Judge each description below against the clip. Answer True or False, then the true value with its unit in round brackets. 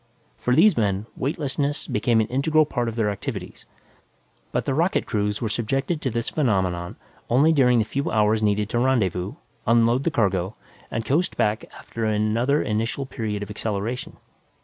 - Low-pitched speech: True (115 Hz)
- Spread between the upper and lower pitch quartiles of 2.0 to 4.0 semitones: False (4.4 semitones)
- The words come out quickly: False (165 wpm)